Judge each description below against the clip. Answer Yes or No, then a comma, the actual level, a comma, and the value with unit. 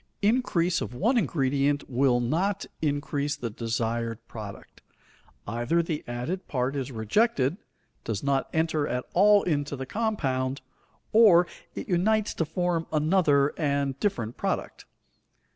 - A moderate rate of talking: No, slow, 125 wpm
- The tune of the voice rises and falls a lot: Yes, wide, 5.8 semitones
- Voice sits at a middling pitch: Yes, medium, 145 Hz